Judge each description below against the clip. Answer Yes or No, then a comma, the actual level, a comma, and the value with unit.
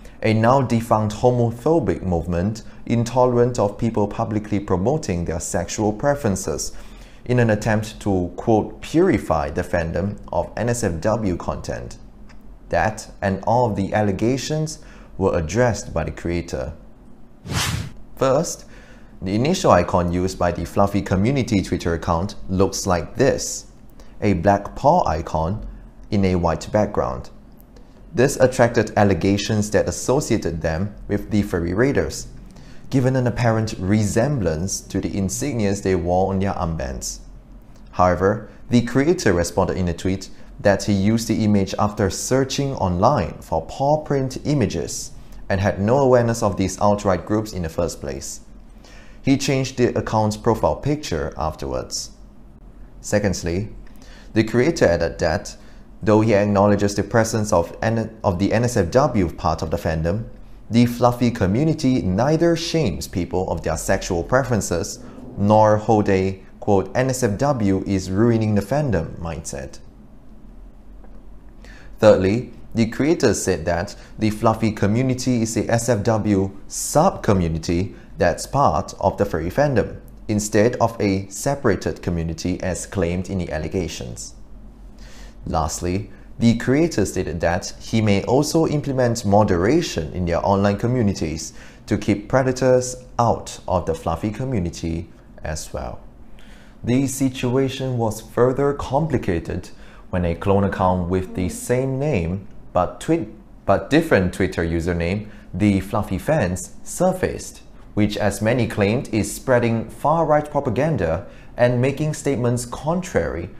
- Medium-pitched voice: No, low, 105 Hz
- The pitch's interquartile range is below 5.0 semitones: Yes, average, 4.4 semitones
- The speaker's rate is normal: No, slow, 130 wpm